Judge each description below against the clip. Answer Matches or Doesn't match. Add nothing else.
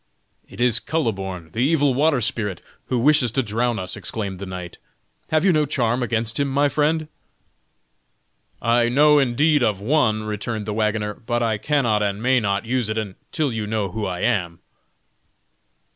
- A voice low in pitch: Matches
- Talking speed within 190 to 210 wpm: Doesn't match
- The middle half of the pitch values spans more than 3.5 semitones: Matches